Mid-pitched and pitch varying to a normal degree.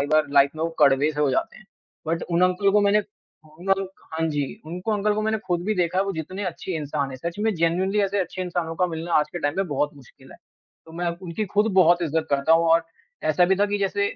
Yes: medium, 175 Hz; average, 3.6 semitones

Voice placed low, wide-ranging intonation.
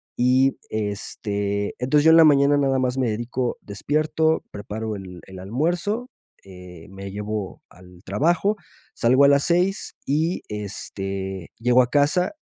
Yes: low, 125 Hz; wide, 6.6 semitones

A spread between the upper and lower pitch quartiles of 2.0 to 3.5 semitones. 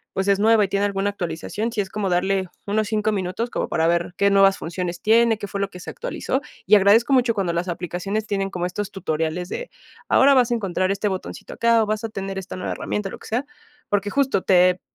Yes: average, 3.0 semitones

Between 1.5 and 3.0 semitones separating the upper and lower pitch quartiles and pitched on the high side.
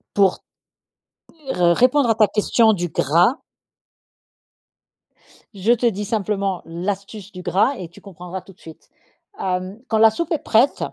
No: average, 3.5 semitones; high, 200 Hz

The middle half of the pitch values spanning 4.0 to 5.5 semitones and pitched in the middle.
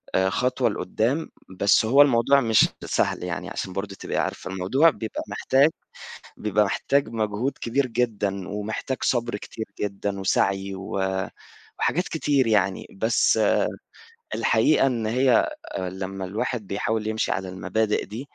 No: average, 4.3 semitones; low, 110 Hz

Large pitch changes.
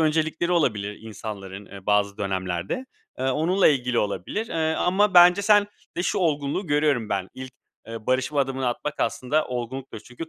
Yes: wide, 7.1 semitones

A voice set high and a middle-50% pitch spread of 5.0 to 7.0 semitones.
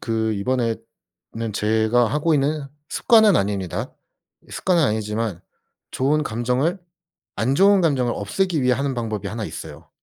No: low, 120 Hz; wide, 5.5 semitones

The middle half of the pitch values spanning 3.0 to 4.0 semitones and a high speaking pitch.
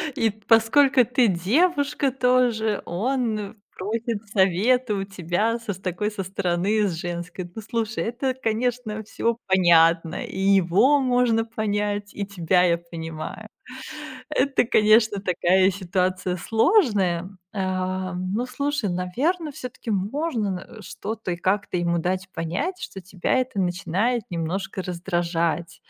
No: average, 4.4 semitones; high, 205 Hz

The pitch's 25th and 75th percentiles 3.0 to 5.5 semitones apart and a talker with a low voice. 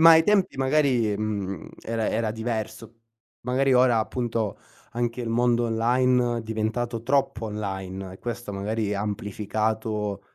No: narrow, 2.4 semitones; low, 115 Hz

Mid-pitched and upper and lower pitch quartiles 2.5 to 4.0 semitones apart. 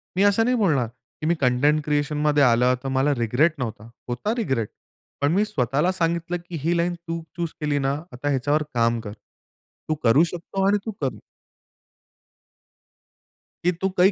No: medium, 150 Hz; wide, 5.4 semitones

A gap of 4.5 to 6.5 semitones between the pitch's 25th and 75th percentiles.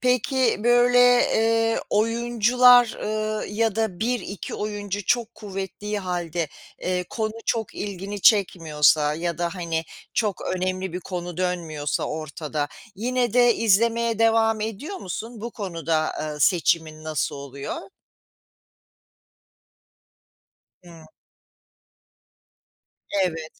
Yes: average, 5.1 semitones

